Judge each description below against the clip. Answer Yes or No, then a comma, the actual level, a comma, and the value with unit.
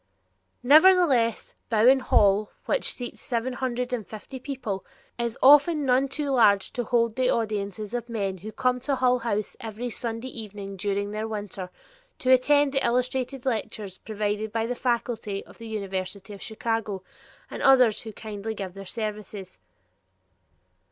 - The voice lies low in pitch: No, high, 225 Hz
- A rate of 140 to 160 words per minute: Yes, average, 150 wpm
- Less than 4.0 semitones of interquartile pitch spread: Yes, average, 3.4 semitones